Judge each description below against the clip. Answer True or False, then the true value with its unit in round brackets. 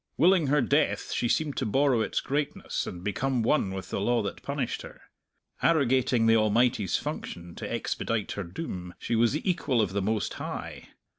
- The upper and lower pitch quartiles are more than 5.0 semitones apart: True (5.5 semitones)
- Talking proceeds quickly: False (180 wpm)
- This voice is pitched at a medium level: False (120 Hz)